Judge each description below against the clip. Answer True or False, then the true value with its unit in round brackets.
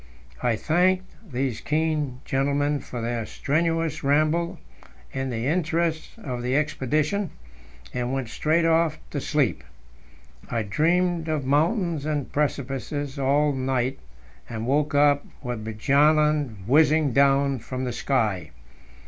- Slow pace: True (125 wpm)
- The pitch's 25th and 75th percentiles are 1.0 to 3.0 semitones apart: False (3.4 semitones)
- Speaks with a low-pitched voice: False (145 Hz)